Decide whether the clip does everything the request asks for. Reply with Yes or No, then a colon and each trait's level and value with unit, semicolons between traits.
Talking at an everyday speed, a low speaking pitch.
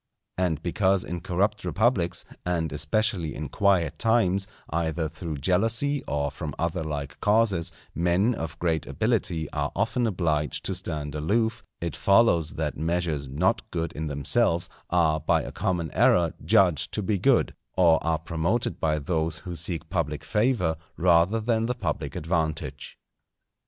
Yes: average, 150 wpm; very low, 85 Hz